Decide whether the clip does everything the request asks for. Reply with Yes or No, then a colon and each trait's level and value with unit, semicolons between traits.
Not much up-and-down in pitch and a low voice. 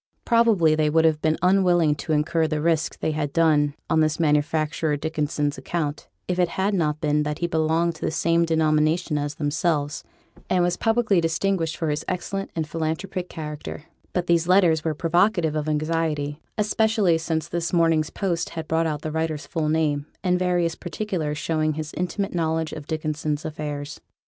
No: narrow, 2.2 semitones; medium, 160 Hz